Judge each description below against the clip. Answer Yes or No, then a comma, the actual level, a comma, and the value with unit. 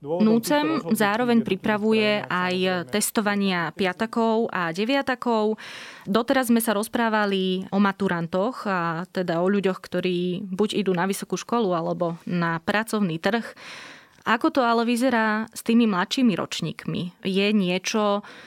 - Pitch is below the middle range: No, high, 205 Hz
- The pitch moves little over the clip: No, average, 3.6 semitones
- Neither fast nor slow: Yes, average, 125 wpm